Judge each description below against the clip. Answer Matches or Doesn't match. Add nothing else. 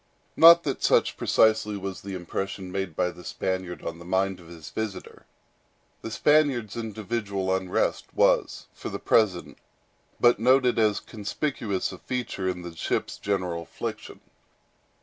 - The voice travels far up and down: Doesn't match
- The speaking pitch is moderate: Doesn't match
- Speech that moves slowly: Doesn't match